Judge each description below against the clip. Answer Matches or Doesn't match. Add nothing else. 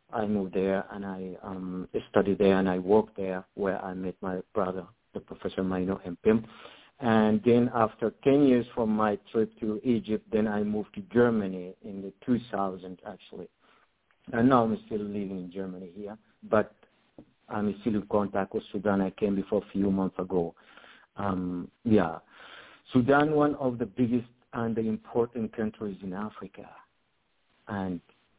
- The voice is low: Matches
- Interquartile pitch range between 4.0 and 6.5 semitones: Doesn't match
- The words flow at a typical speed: Matches